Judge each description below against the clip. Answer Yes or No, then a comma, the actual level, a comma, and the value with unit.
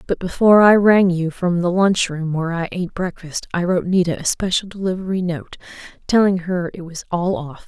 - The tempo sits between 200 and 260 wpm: Yes, fast, 205 wpm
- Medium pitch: Yes, medium, 180 Hz